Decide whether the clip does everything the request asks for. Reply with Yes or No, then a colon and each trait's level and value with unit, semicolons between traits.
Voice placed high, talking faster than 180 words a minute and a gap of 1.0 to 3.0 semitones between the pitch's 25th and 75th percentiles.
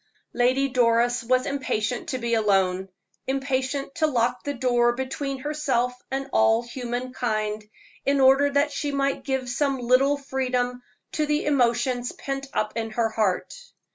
No: very high, 255 Hz; average, 150 wpm; narrow, 2.5 semitones